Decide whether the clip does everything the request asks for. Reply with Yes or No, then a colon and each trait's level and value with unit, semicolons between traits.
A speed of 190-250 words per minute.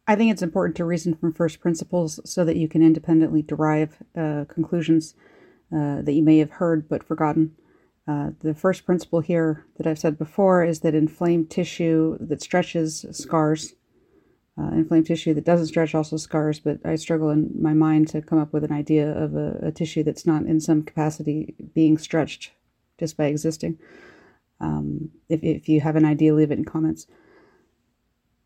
No: average, 180 wpm